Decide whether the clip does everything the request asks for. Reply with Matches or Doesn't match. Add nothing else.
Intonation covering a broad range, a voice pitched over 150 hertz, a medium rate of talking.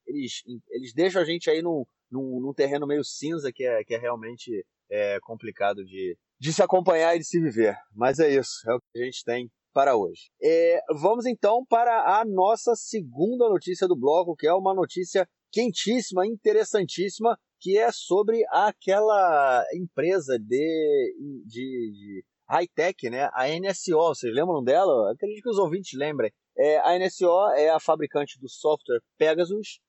Matches